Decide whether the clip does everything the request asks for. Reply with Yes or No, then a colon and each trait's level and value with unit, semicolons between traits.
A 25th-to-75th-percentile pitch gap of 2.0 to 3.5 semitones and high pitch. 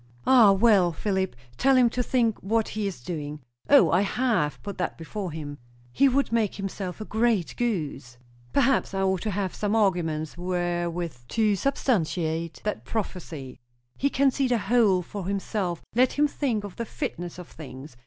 No: average, 5.2 semitones; high, 195 Hz